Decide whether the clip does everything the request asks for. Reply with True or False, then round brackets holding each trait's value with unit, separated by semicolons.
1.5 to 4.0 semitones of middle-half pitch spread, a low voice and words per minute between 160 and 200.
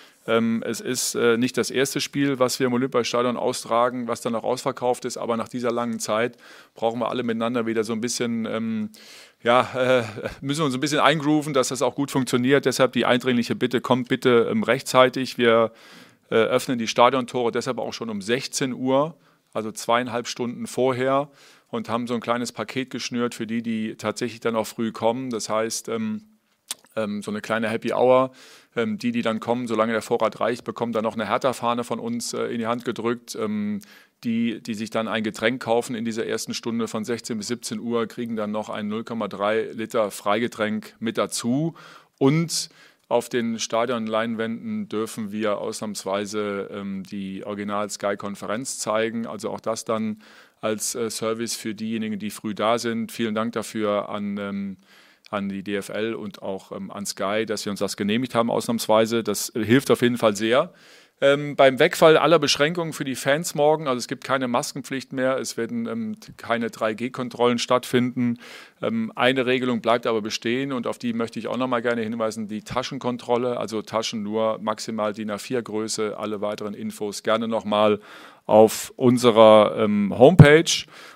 True (2.6 semitones; 115 Hz; 170 wpm)